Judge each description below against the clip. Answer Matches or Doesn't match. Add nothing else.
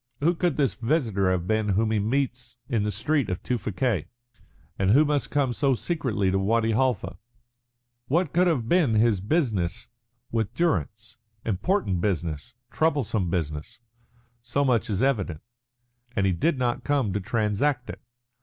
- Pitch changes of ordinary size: Doesn't match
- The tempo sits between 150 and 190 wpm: Matches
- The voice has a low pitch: Matches